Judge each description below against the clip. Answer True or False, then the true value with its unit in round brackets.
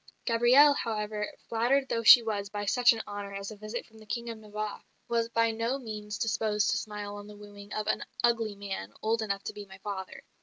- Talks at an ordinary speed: False (220 wpm)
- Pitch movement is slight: True (2.0 semitones)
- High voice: True (215 Hz)